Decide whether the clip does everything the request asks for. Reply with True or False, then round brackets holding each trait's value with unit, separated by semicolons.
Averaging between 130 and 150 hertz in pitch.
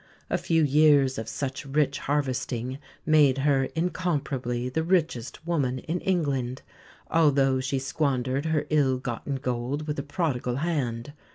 True (140 Hz)